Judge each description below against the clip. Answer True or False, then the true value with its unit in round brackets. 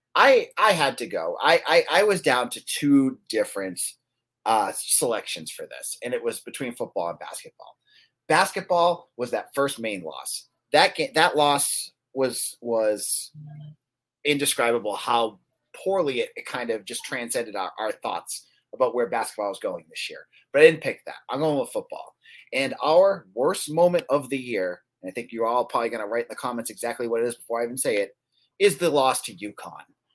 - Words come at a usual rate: True (195 wpm)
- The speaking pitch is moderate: True (150 Hz)